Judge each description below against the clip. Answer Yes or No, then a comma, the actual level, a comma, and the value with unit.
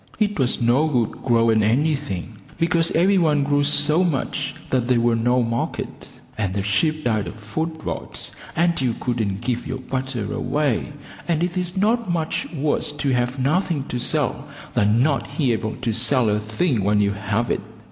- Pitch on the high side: No, low, 130 Hz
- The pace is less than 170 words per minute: No, average, 180 wpm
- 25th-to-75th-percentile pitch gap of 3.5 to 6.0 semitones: Yes, average, 5.3 semitones